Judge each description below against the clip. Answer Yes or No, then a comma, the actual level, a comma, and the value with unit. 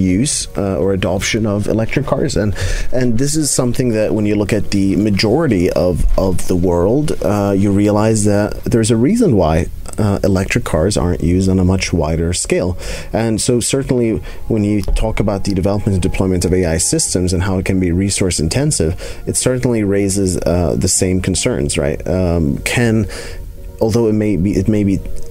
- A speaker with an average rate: Yes, average, 185 wpm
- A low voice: Yes, very low, 95 Hz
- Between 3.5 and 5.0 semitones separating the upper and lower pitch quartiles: No, average, 2.9 semitones